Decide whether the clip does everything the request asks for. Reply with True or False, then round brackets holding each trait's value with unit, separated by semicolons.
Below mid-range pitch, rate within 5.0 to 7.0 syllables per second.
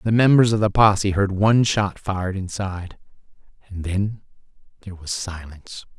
True (100 Hz; 5.4 syllables/s)